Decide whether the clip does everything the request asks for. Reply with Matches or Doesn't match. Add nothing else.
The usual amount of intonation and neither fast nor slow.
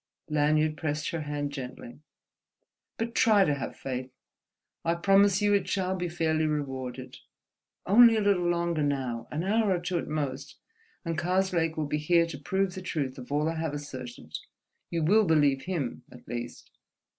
Matches